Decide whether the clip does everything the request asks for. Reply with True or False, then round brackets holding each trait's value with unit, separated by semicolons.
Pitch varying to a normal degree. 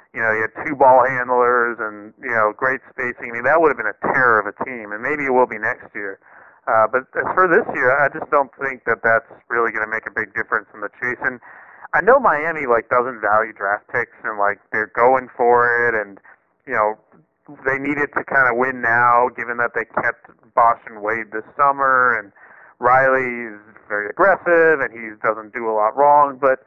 True (3.1 semitones)